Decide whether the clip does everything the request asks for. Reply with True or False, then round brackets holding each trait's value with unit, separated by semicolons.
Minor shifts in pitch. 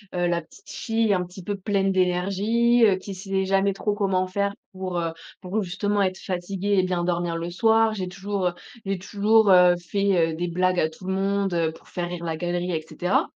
True (2.2 semitones)